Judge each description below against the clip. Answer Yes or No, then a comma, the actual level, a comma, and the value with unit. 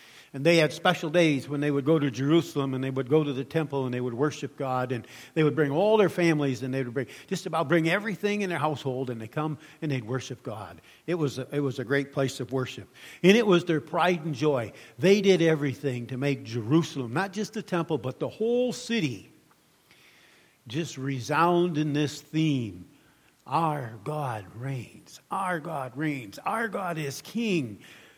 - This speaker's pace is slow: No, average, 200 wpm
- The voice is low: No, medium, 145 Hz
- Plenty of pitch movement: No, average, 4.2 semitones